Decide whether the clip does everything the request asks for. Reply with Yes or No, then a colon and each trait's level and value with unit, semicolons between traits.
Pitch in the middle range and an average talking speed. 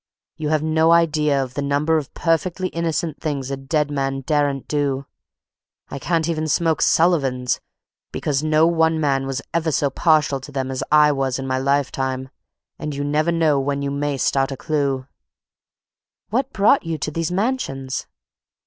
Yes: medium, 145 Hz; average, 170 wpm